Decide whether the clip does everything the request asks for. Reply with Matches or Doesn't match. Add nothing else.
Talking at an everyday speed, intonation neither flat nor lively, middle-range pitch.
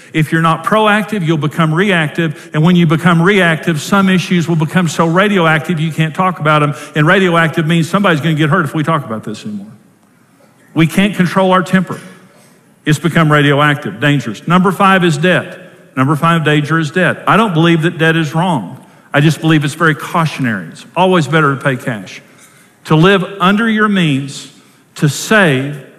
Matches